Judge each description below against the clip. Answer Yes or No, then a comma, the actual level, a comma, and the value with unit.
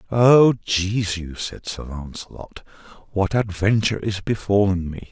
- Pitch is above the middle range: No, low, 100 Hz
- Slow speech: Yes, slow, 115 wpm